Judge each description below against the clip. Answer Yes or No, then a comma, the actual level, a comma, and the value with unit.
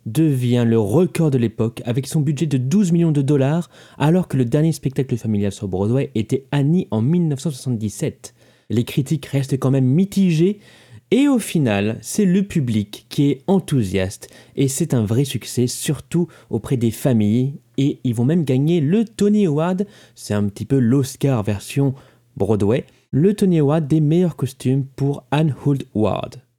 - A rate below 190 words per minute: Yes, average, 165 wpm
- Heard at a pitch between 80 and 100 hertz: No, low, 135 Hz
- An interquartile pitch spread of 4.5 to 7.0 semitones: Yes, average, 4.9 semitones